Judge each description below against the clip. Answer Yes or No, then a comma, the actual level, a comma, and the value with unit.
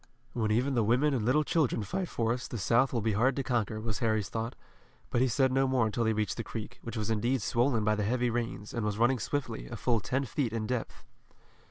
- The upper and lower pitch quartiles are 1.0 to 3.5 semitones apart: Yes, average, 2.9 semitones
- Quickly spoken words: Yes, fast, 245 wpm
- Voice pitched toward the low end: Yes, low, 115 Hz